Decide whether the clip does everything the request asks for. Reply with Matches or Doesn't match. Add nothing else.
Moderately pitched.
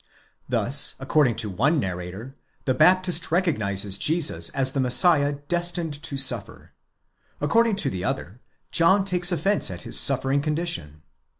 Matches